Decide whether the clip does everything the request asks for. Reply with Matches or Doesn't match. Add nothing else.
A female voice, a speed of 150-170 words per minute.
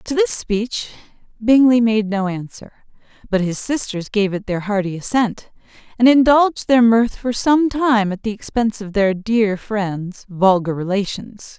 Matches